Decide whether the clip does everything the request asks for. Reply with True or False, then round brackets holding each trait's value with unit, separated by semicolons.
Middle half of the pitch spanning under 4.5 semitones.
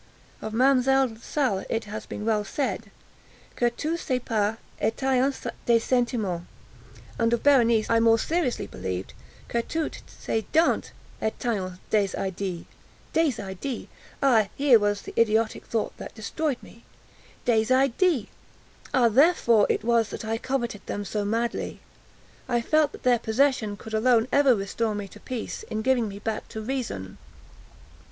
True (3.4 semitones)